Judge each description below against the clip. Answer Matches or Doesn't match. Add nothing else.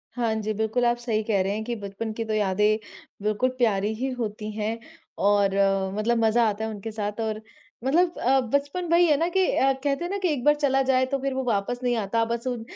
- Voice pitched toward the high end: Matches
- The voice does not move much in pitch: Doesn't match